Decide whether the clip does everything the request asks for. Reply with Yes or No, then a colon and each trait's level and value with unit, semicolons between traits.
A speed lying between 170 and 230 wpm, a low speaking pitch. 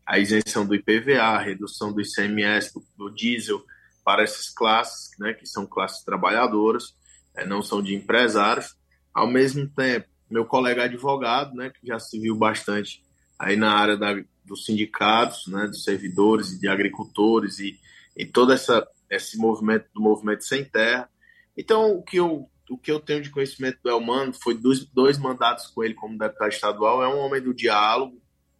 Yes: average, 175 wpm; low, 110 Hz